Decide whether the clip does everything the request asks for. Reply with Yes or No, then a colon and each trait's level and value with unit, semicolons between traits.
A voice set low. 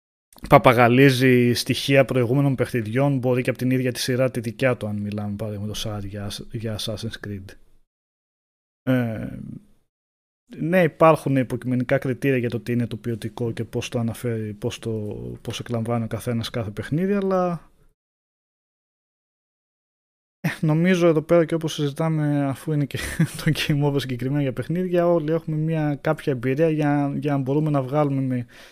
Yes: low, 130 Hz